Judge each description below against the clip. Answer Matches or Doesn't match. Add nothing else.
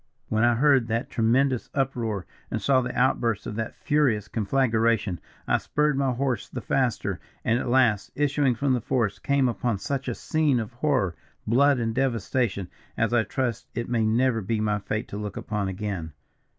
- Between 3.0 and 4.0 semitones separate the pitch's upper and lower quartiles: Matches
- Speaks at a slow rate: Doesn't match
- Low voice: Matches